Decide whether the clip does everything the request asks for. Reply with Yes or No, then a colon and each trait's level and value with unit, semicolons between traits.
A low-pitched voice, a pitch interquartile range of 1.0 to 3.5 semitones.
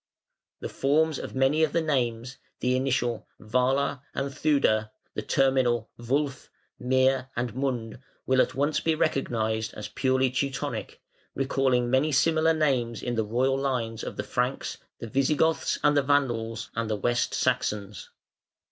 Yes: low, 130 Hz; average, 3.0 semitones